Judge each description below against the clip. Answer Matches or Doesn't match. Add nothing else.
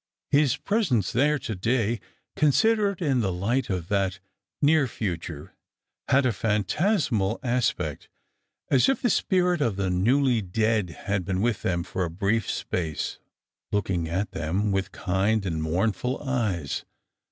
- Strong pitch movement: Matches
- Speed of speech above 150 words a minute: Doesn't match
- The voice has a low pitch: Matches